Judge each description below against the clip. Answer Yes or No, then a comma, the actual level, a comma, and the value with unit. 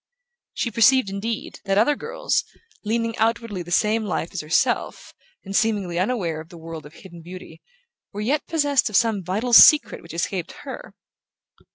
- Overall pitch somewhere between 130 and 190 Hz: No, high, 205 Hz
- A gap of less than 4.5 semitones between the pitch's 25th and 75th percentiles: No, average, 4.8 semitones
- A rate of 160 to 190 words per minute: Yes, average, 165 wpm